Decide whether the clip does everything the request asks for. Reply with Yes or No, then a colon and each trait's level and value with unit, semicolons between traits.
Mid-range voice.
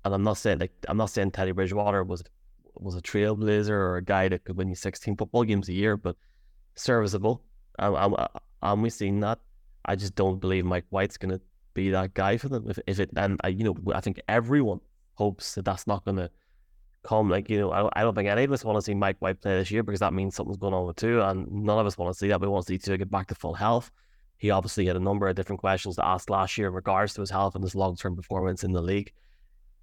No: low, 100 Hz